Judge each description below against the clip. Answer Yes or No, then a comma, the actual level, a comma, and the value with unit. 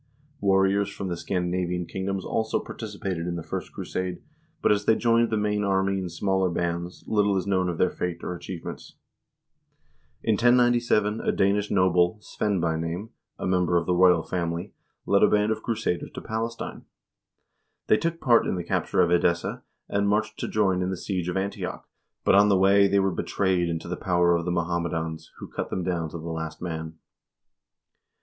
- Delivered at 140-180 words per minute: No, average, 190 wpm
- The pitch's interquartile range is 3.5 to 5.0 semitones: No, average, 2.8 semitones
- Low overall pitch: Yes, very low, 95 Hz